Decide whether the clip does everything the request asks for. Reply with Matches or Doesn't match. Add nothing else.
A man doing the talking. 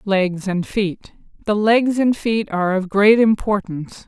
Doesn't match